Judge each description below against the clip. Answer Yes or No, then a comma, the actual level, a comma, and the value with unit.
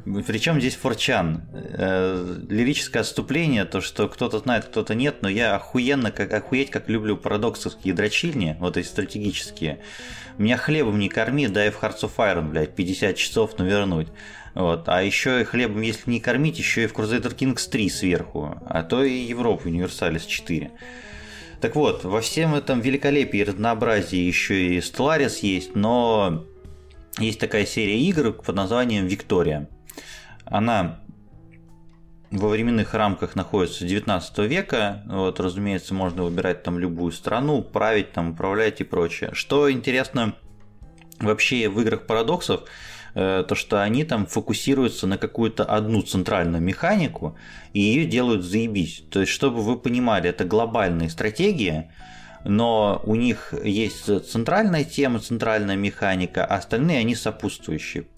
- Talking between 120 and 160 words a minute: Yes, average, 140 wpm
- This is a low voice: Yes, low, 105 Hz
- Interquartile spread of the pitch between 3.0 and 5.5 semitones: Yes, average, 4.4 semitones